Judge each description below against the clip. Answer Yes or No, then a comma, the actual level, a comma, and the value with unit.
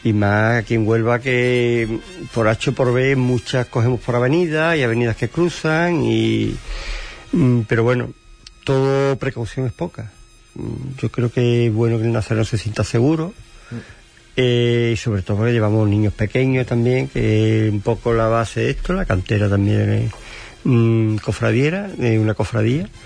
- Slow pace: No, average, 165 wpm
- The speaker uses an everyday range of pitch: No, narrow, 2.3 semitones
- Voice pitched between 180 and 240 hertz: No, low, 115 Hz